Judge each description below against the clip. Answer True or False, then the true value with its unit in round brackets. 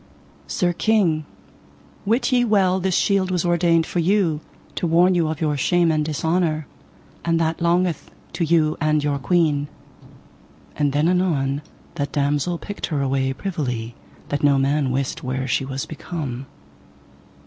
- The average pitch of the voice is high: False (160 Hz)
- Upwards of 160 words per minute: False (150 wpm)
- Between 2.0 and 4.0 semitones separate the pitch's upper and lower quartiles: True (3.7 semitones)